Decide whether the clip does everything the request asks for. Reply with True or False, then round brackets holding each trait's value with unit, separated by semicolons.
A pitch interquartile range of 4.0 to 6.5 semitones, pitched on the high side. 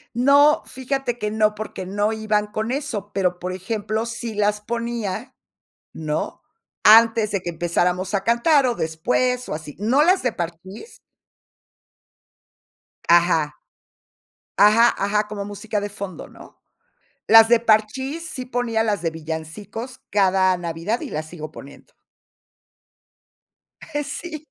True (4.3 semitones; 210 Hz)